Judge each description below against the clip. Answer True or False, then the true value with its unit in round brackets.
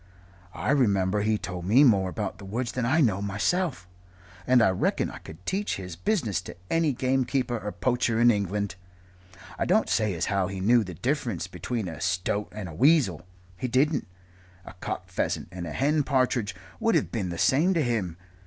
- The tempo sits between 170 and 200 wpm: True (190 wpm)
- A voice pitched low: True (110 Hz)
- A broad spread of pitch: True (5.7 semitones)